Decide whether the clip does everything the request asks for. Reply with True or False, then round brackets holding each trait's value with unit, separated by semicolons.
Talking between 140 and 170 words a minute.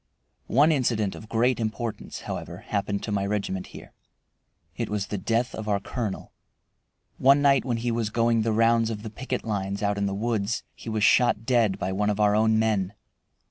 False (195 wpm)